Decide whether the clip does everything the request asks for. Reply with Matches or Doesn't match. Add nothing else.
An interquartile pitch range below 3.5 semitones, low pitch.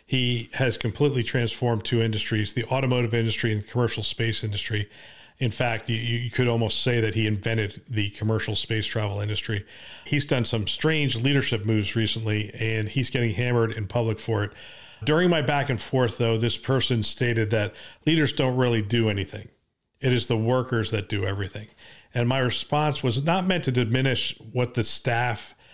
Matches